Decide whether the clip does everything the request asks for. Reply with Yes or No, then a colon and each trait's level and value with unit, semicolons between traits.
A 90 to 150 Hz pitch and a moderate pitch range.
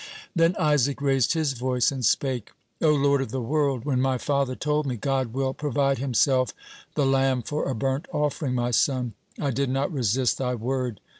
No: low, 135 Hz; narrow, 2.1 semitones